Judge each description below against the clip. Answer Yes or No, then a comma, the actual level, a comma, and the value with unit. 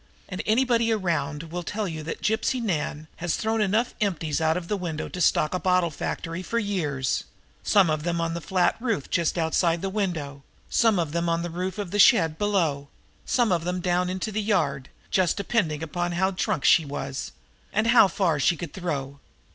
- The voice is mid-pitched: Yes, medium, 175 Hz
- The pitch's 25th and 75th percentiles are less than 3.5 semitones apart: No, average, 4.1 semitones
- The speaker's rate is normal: No, fast, 210 wpm